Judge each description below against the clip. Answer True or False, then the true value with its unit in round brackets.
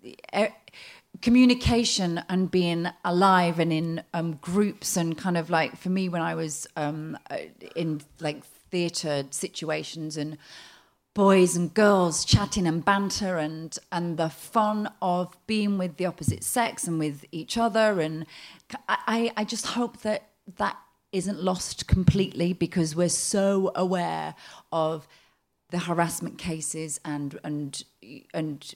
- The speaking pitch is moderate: True (175 Hz)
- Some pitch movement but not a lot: True (3.3 semitones)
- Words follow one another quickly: False (135 wpm)